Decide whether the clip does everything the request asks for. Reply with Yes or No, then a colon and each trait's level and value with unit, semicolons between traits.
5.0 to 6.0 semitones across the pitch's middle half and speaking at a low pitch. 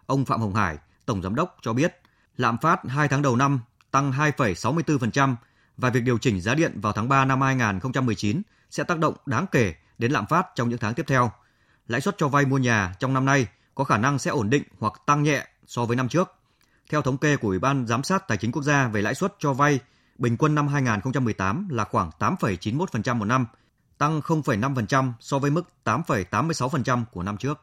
No: average, 4.2 semitones; low, 130 Hz